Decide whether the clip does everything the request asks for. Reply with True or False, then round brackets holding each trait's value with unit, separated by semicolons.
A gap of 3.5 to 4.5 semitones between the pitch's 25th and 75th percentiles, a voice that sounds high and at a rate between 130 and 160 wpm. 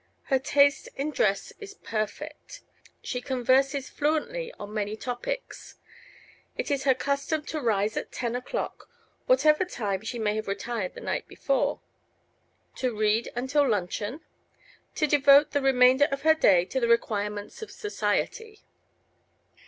False (5.6 semitones; 265 Hz; 140 wpm)